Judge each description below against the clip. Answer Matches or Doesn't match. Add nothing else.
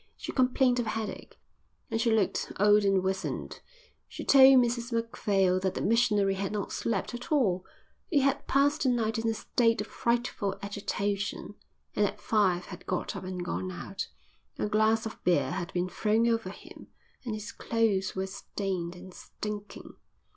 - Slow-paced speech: Doesn't match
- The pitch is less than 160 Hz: Doesn't match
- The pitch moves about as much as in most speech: Matches